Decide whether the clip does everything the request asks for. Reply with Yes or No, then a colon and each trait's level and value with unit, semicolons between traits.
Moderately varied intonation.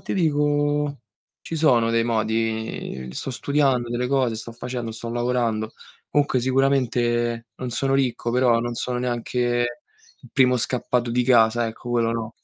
No: narrow, 2.0 semitones